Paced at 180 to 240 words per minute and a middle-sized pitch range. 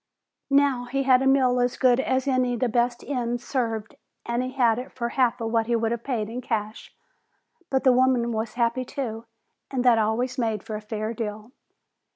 No: average, 200 wpm; narrow, 2.1 semitones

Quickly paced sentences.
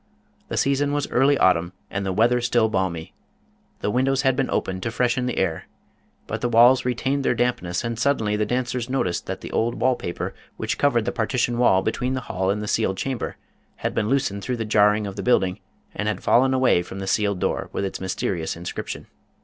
Yes: fast, 210 wpm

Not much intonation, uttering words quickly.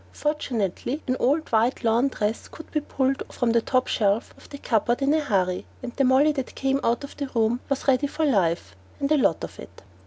No: average, 3.7 semitones; fast, 220 wpm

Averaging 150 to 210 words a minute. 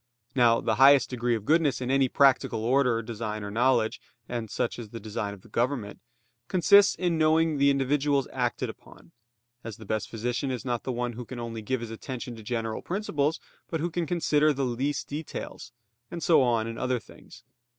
Yes: average, 190 wpm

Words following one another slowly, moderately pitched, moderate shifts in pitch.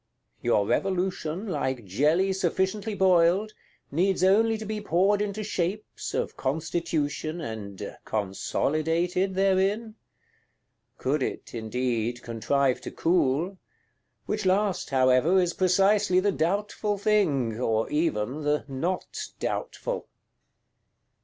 No: slow, 105 wpm; medium, 175 Hz; wide, 6.5 semitones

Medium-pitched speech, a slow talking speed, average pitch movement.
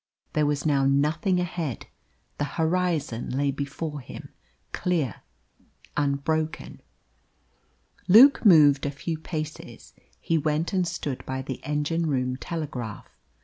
Yes: medium, 150 Hz; slow, 115 wpm; average, 3.0 semitones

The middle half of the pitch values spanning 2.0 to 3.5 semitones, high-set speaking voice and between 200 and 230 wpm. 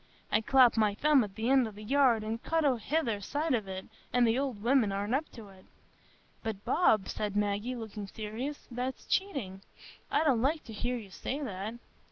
No: average, 4.4 semitones; high, 230 Hz; fast, 205 wpm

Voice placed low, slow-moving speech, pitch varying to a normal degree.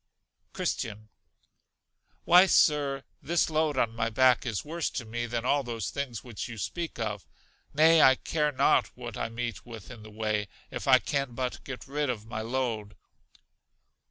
No: low, 120 Hz; average, 170 wpm; average, 4.1 semitones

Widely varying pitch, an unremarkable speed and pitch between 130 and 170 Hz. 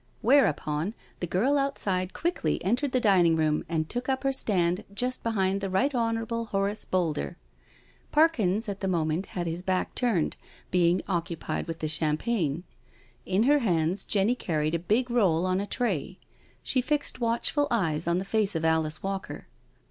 No: wide, 5.7 semitones; average, 170 wpm; high, 190 Hz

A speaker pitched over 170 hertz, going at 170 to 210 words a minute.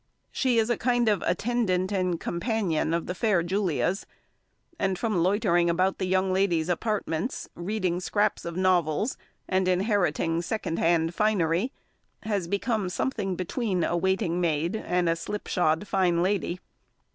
No: medium, 185 Hz; average, 145 wpm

